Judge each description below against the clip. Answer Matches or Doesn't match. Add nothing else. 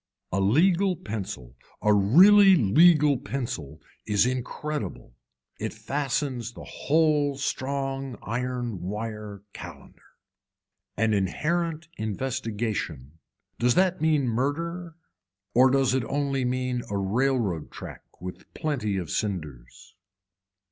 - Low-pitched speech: Matches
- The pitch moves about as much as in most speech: Doesn't match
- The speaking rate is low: Matches